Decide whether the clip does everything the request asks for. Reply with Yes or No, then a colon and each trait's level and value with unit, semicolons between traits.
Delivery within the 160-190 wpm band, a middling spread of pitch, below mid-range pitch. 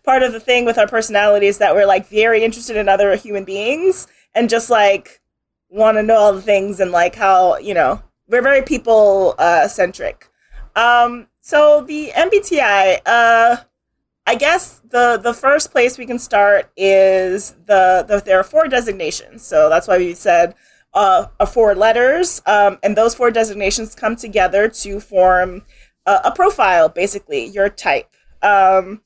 No: average, 170 wpm; average, 3.7 semitones; high, 220 Hz